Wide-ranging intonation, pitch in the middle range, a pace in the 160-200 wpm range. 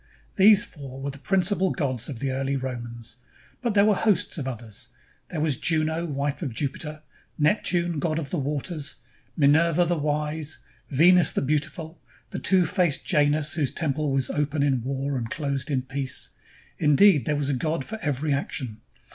No: average, 3.5 semitones; medium, 150 Hz; average, 175 wpm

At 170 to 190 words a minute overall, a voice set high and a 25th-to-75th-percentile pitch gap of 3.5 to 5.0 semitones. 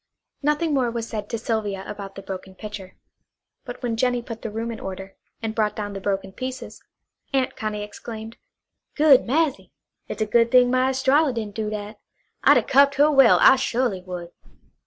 Yes: average, 185 wpm; high, 225 Hz; average, 3.9 semitones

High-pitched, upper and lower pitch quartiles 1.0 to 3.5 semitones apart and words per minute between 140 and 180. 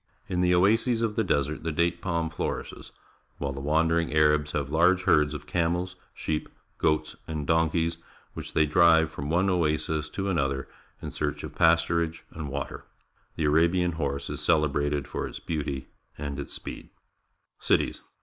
No: very low, 80 Hz; narrow, 2.4 semitones; average, 165 wpm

